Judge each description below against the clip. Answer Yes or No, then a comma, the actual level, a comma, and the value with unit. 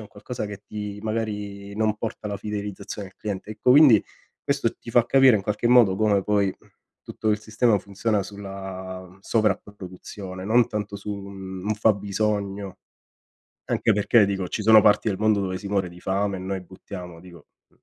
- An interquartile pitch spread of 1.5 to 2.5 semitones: Yes, narrow, 1.9 semitones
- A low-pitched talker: Yes, low, 100 Hz